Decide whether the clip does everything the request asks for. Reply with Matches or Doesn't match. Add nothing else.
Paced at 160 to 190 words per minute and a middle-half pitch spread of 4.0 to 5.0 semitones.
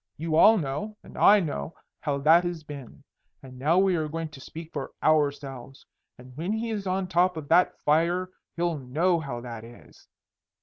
Matches